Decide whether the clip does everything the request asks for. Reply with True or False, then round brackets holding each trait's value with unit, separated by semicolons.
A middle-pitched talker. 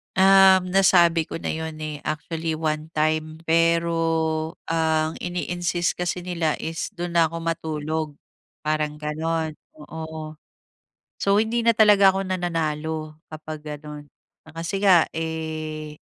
True (160 Hz)